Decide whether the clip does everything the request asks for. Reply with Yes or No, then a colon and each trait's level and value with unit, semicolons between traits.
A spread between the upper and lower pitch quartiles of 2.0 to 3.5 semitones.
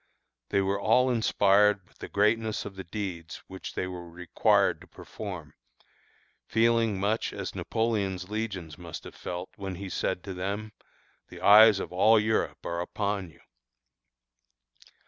Yes: average, 3.0 semitones